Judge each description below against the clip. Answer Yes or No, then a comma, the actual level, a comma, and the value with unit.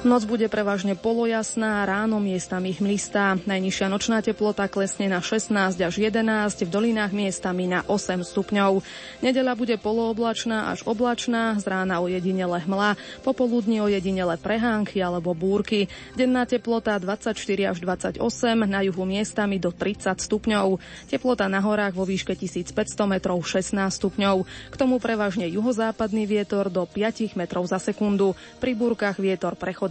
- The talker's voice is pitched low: No, high, 205 Hz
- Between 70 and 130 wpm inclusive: No, average, 140 wpm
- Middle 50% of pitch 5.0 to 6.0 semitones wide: No, average, 2.8 semitones